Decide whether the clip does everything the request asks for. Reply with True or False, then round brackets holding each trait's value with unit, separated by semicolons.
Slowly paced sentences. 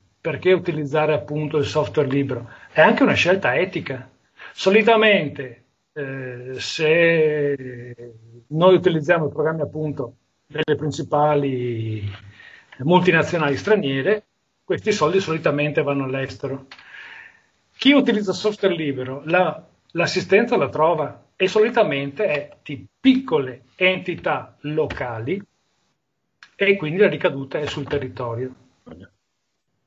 True (100 wpm)